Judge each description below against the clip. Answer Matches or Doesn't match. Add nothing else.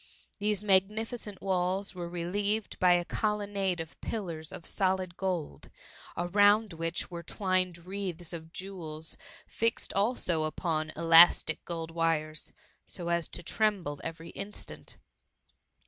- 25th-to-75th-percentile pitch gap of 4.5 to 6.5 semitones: Doesn't match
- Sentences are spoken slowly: Matches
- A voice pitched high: Doesn't match